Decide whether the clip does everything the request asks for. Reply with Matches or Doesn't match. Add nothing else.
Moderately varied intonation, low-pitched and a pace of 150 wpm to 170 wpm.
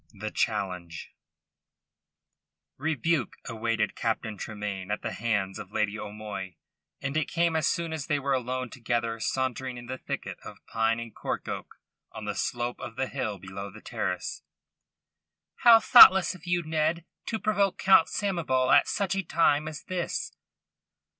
Doesn't match